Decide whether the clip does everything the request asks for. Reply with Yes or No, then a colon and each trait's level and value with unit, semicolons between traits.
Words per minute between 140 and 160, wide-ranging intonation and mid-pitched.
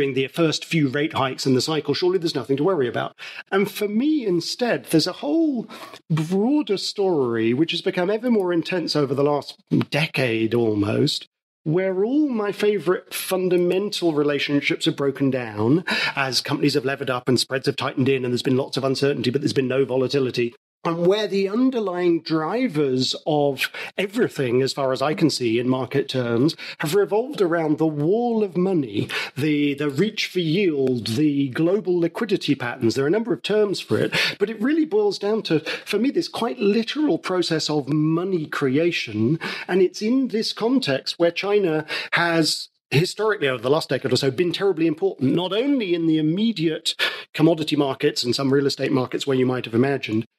No: average, 185 wpm; wide, 6.1 semitones; medium, 160 Hz